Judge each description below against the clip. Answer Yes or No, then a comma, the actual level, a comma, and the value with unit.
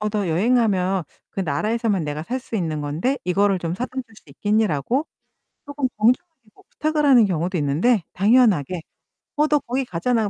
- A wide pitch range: Yes, wide, 6.1 semitones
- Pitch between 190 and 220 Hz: Yes, high, 210 Hz